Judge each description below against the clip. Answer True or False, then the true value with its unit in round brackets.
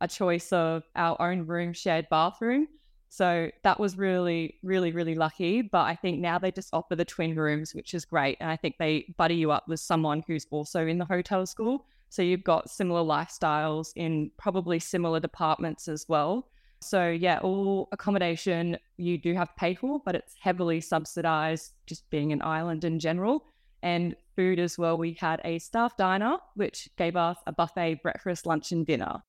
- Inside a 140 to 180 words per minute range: False (190 wpm)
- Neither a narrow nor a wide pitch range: False (2.3 semitones)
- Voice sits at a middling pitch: True (170 Hz)